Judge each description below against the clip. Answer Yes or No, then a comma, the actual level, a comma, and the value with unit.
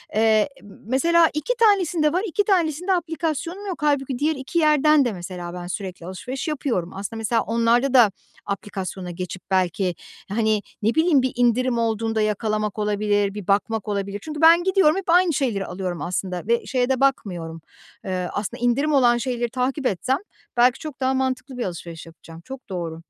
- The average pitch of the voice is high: Yes, high, 240 Hz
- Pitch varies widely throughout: Yes, wide, 6.8 semitones